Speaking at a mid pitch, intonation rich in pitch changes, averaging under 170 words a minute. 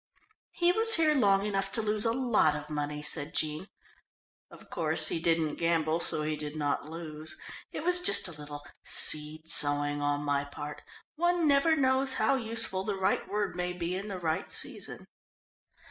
No: medium, 170 Hz; wide, 7.1 semitones; average, 175 wpm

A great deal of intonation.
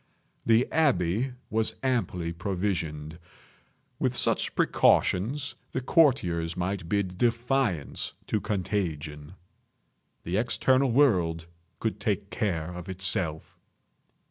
Yes: wide, 5.7 semitones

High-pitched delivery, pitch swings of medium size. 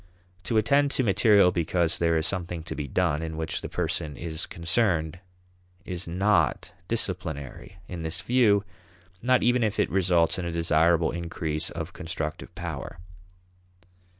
No: very low, 85 Hz; average, 3.5 semitones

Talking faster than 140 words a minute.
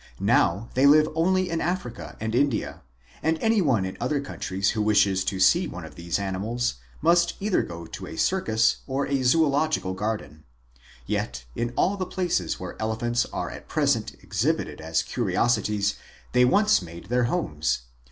Yes: average, 170 wpm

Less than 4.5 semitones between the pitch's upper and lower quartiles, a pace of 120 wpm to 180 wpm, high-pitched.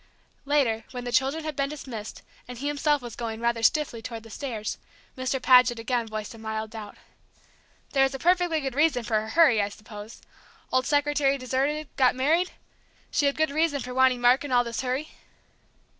No: average, 4.0 semitones; average, 190 wpm; very high, 255 Hz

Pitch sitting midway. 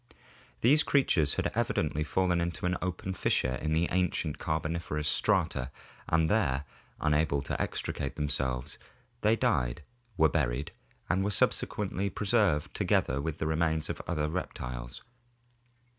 No: very low, 80 Hz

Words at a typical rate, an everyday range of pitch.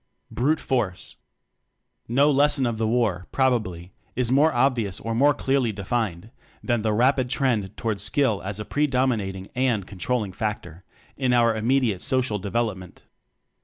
Yes: average, 155 wpm; average, 4.4 semitones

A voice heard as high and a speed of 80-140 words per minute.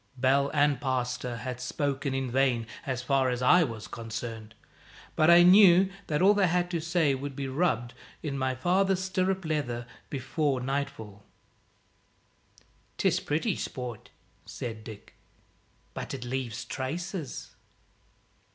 No: low, 135 Hz; slow, 135 wpm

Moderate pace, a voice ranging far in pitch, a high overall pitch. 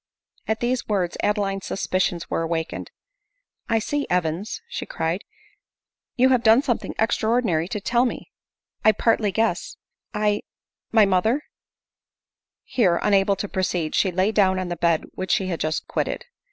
No: average, 165 wpm; average, 3.9 semitones; high, 200 Hz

